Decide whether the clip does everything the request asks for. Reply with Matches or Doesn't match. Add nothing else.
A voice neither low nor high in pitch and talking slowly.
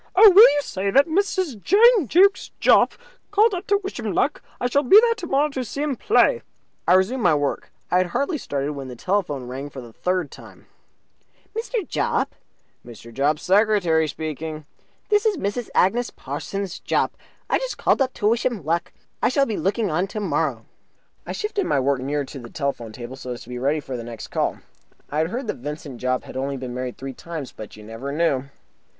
Doesn't match